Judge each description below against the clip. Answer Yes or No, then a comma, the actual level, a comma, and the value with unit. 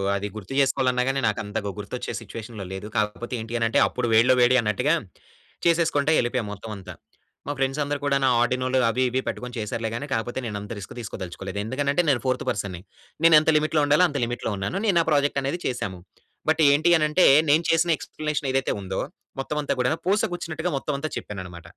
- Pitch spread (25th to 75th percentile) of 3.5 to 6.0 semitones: Yes, wide, 5.4 semitones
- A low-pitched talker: Yes, low, 130 Hz